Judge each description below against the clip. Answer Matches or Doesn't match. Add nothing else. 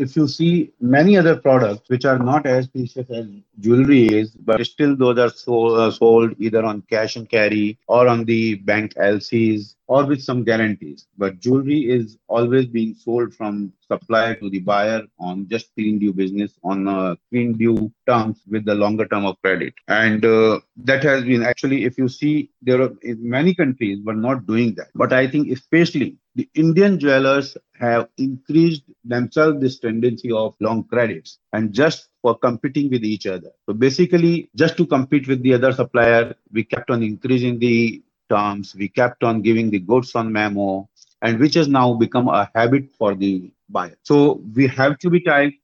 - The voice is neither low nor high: Doesn't match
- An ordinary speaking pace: Matches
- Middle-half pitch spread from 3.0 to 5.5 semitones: Matches